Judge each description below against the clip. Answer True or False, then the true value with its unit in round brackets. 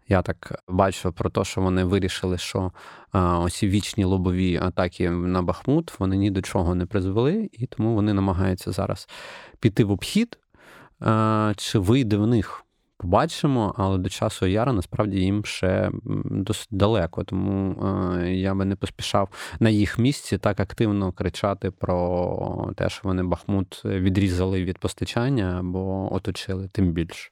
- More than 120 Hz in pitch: False (95 Hz)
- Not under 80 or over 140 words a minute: False (150 wpm)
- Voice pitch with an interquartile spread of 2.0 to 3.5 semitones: True (2.5 semitones)